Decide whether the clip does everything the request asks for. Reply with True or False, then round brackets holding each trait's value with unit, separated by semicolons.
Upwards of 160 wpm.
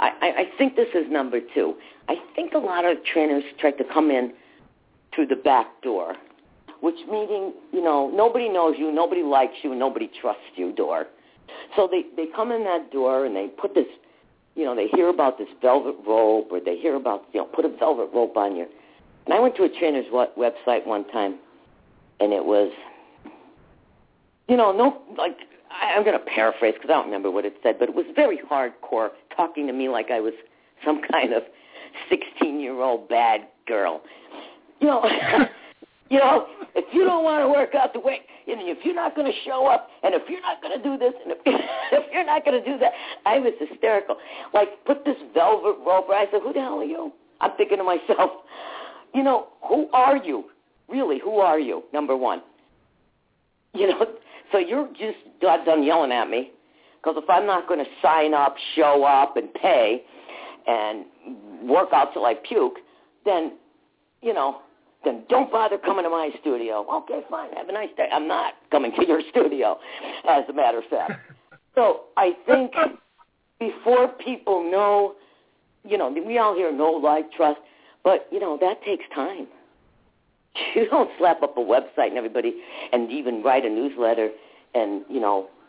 True (190 wpm)